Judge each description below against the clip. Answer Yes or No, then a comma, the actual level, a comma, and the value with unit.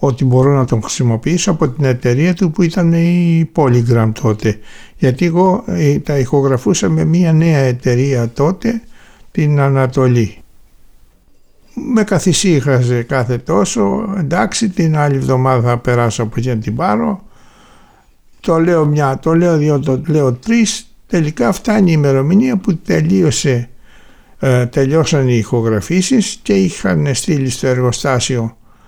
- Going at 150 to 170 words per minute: No, average, 130 wpm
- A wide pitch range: Yes, wide, 5.9 semitones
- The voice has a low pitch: No, medium, 145 Hz